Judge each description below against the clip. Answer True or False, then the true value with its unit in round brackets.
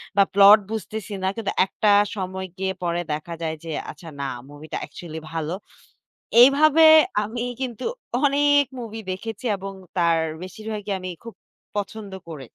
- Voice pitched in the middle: False (200 Hz)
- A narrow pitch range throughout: False (4.6 semitones)